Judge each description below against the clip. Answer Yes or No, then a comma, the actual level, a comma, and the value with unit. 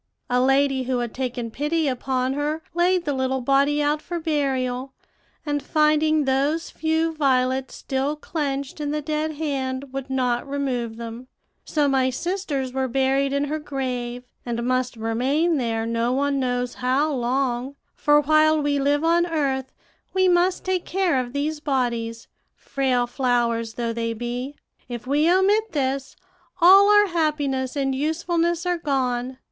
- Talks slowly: No, average, 155 wpm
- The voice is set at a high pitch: Yes, very high, 275 Hz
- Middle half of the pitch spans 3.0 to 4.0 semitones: Yes, average, 3.4 semitones